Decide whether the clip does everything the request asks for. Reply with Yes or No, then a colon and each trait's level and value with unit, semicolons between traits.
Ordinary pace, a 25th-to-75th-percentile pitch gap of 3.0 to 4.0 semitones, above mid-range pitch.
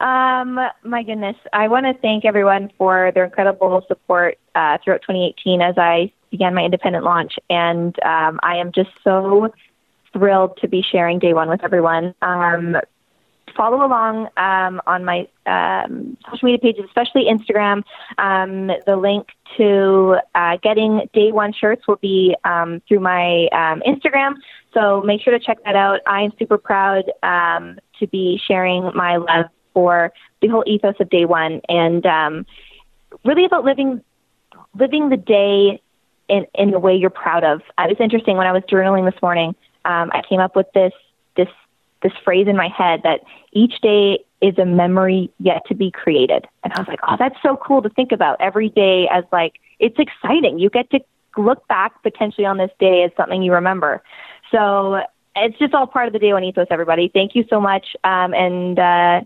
Yes: average, 185 wpm; average, 3.6 semitones; high, 195 Hz